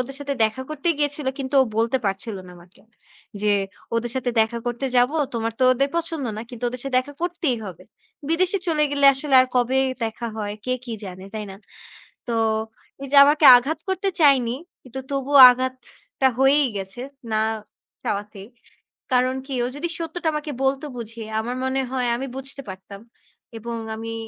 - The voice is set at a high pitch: Yes, very high, 255 Hz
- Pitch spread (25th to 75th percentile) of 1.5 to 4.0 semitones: Yes, average, 3.7 semitones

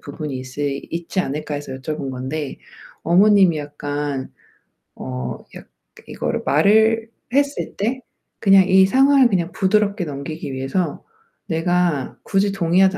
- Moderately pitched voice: Yes, medium, 170 Hz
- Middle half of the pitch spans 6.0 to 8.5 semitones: No, wide, 5.4 semitones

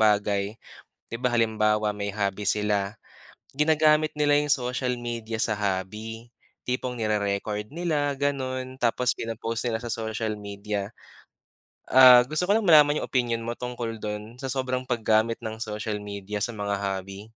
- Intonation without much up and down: No, average, 3.4 semitones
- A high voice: No, low, 115 Hz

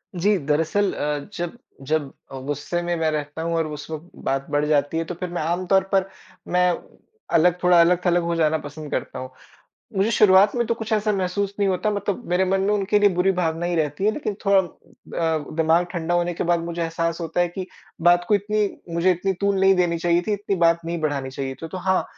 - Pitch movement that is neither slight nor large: Yes, average, 3.0 semitones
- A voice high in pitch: No, medium, 175 Hz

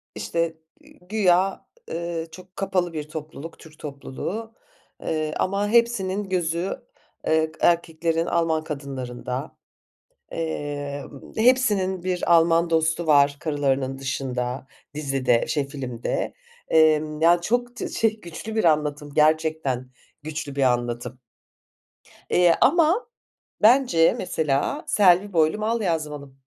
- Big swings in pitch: No, average, 4.4 semitones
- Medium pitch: Yes, medium, 160 Hz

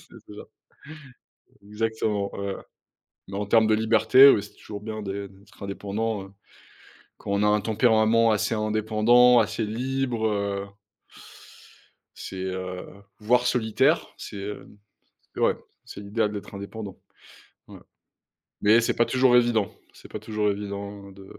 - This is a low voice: Yes, low, 105 Hz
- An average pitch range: No, narrow, 2.0 semitones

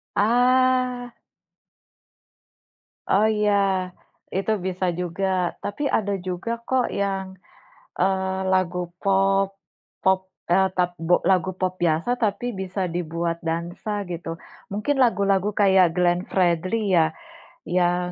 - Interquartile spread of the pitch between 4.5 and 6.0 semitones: No, narrow, 2.6 semitones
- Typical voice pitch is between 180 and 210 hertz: Yes, high, 190 Hz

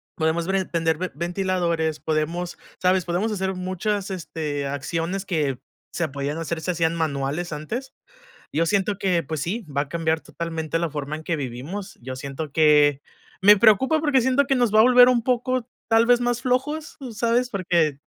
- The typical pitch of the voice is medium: Yes, medium, 175 Hz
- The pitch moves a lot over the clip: Yes, wide, 5.7 semitones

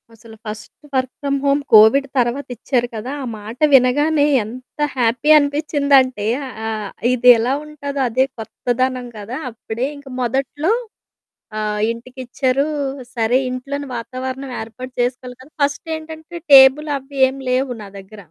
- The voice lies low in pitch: No, very high, 255 Hz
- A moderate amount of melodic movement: Yes, average, 3.2 semitones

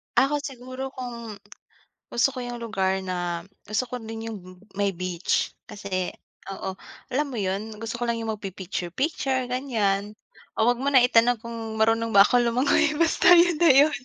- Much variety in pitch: No, average, 4.2 semitones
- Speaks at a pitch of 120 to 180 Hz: No, high, 230 Hz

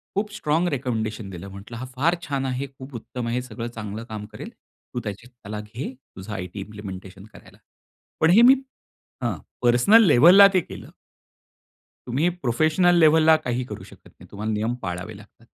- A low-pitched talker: Yes, low, 120 Hz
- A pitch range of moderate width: No, wide, 6.4 semitones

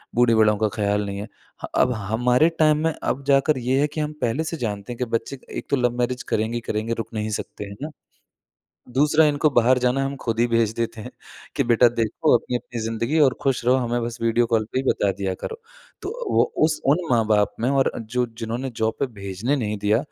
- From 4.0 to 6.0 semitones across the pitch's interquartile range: No, average, 3.2 semitones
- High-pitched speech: No, low, 120 Hz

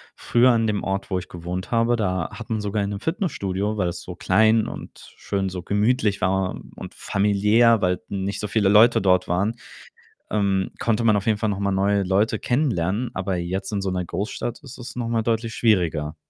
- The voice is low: Yes, low, 100 Hz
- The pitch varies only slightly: No, average, 3.1 semitones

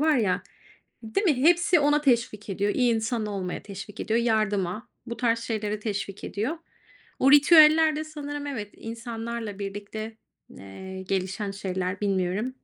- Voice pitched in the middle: No, high, 220 Hz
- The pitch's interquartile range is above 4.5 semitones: Yes, average, 4.9 semitones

